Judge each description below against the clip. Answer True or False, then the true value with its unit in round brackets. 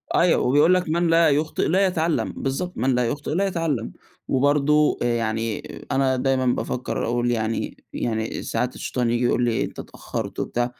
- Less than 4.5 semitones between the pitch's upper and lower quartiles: False (4.8 semitones)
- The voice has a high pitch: False (135 Hz)